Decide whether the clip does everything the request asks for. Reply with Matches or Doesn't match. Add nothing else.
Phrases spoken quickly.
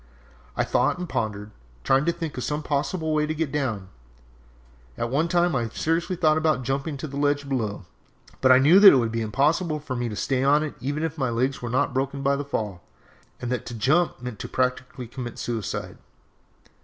Matches